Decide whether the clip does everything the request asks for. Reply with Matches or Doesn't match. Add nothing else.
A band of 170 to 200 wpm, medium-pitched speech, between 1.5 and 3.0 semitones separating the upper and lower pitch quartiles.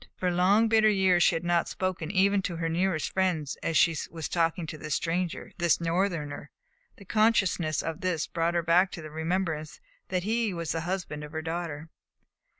Matches